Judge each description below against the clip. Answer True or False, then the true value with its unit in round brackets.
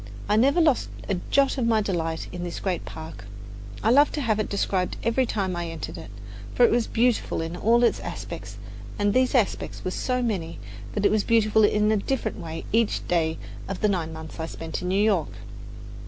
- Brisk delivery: True (210 wpm)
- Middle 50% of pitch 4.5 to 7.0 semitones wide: True (5.1 semitones)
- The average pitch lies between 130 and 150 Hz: False (205 Hz)